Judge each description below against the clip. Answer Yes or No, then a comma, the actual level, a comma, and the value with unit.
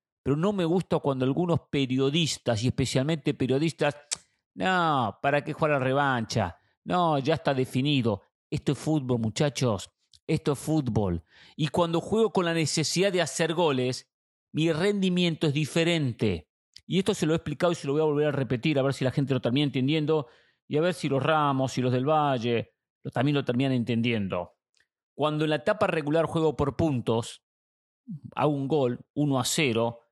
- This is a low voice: No, medium, 145 Hz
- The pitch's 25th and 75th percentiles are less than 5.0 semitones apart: Yes, average, 4.0 semitones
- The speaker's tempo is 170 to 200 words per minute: Yes, average, 185 wpm